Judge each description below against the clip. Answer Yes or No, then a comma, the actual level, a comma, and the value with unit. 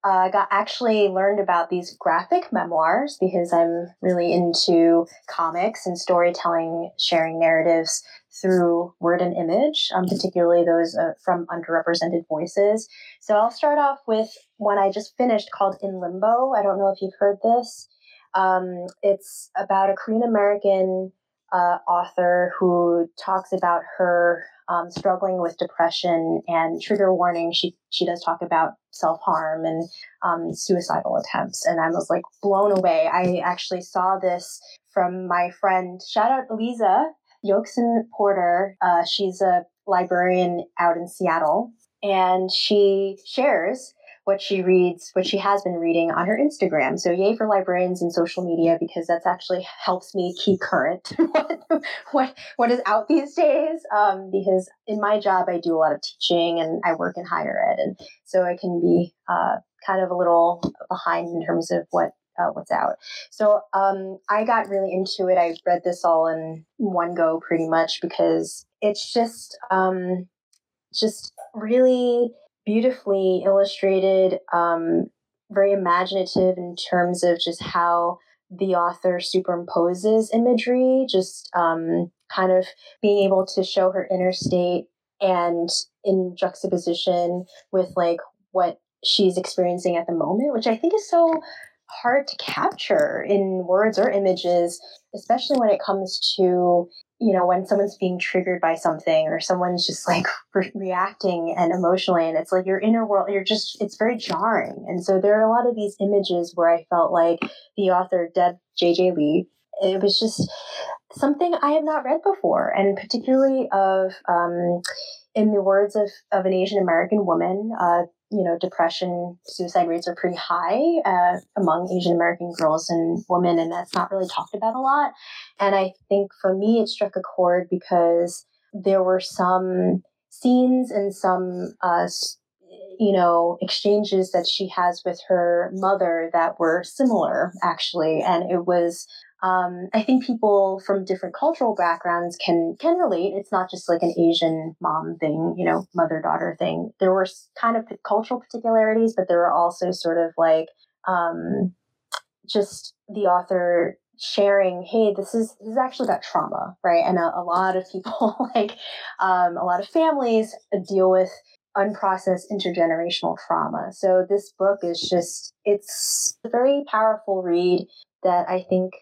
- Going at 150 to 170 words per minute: Yes, average, 160 wpm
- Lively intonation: No, average, 3.0 semitones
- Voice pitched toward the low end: No, medium, 185 Hz